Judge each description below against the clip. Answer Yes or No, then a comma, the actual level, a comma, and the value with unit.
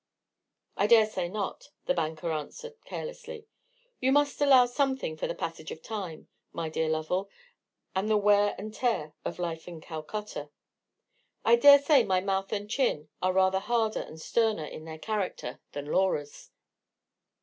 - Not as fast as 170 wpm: Yes, average, 160 wpm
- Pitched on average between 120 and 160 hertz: No, high, 195 Hz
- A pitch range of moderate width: No, wide, 6.3 semitones